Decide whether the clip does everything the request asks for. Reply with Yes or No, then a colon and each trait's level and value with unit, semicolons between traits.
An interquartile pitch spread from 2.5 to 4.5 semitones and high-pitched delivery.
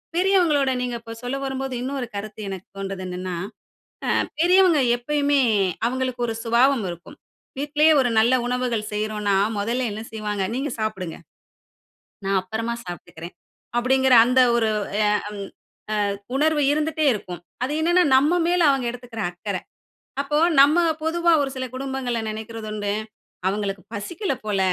No: average, 5.2 semitones; high, 245 Hz